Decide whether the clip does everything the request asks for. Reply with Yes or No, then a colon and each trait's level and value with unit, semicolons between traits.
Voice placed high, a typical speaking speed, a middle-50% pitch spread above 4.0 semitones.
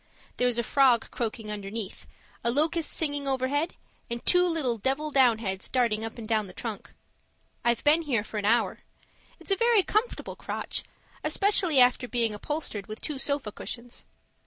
Yes: high, 245 Hz; average, 160 wpm; average, 5.0 semitones